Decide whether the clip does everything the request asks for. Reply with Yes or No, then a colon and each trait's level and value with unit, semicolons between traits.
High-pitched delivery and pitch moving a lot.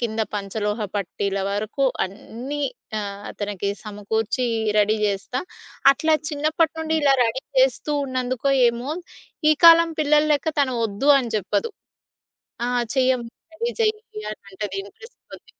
Yes: high, 245 Hz; wide, 6.0 semitones